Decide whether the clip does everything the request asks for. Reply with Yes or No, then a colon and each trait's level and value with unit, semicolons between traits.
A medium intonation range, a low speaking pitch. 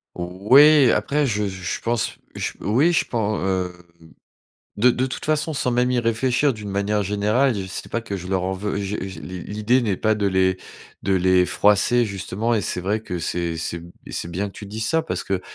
Yes: average, 4.2 semitones; low, 105 Hz